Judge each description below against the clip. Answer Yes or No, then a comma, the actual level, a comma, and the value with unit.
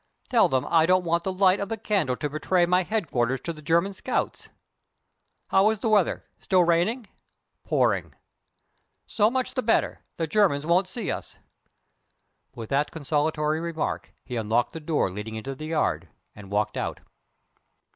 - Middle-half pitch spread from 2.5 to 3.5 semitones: No, average, 5.1 semitones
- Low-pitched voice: No, medium, 165 Hz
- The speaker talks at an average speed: Yes, average, 165 wpm